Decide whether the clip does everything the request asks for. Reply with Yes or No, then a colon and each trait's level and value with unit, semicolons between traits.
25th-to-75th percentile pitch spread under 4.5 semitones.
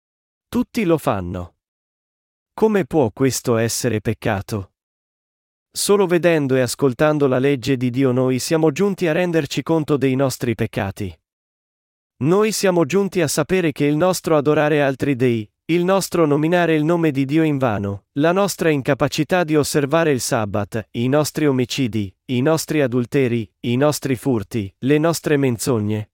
No: average, 5.3 semitones